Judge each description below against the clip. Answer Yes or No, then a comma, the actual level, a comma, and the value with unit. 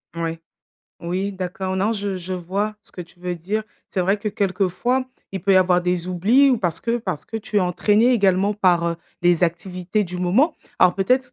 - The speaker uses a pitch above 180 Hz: Yes, high, 190 Hz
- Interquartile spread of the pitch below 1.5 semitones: No, average, 2.9 semitones